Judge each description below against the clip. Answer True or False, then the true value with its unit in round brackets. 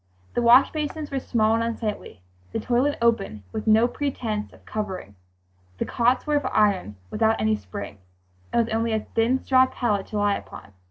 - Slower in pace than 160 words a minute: False (180 wpm)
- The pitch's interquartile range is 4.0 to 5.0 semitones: False (3.0 semitones)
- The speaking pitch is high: True (225 Hz)